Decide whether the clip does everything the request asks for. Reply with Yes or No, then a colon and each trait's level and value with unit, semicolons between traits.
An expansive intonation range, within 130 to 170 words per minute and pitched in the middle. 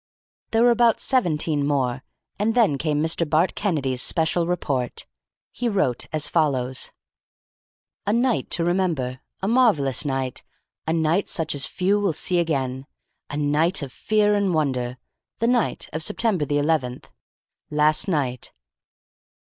Yes: wide, 6.0 semitones; average, 140 wpm; medium, 160 Hz